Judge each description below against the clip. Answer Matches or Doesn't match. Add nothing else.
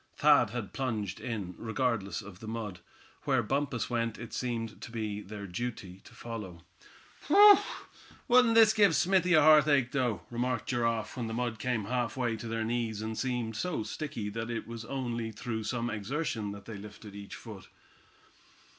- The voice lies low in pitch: Matches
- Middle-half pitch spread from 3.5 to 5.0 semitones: Doesn't match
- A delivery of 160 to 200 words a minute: Matches